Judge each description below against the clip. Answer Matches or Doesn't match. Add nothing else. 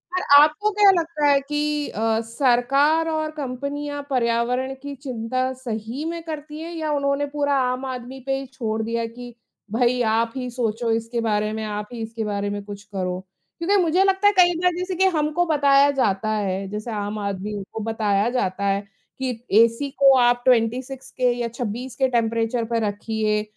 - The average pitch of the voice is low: Doesn't match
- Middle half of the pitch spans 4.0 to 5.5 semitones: Matches